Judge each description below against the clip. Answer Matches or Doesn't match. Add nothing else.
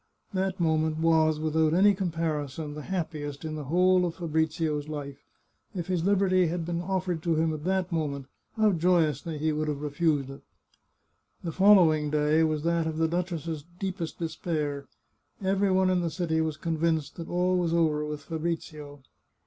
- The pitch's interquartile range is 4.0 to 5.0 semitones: Doesn't match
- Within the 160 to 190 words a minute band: Matches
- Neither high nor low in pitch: Matches